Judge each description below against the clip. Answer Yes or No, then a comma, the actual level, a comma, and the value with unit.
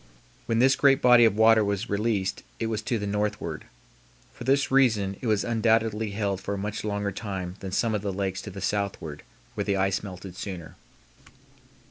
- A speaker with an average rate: Yes, average, 190 wpm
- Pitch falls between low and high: No, low, 105 Hz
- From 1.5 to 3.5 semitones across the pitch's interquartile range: Yes, narrow, 2.5 semitones